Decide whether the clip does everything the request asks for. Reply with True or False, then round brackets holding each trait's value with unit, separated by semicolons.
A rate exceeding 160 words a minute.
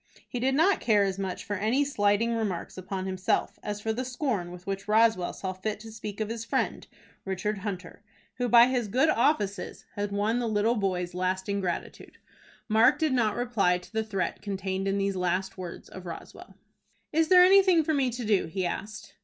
True (195 wpm)